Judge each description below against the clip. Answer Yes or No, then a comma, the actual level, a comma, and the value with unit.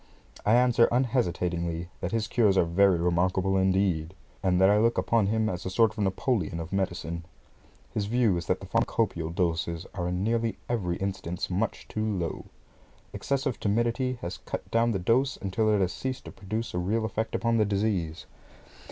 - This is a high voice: No, low, 100 Hz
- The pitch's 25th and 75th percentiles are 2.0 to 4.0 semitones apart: No, average, 4.4 semitones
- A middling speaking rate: Yes, average, 180 wpm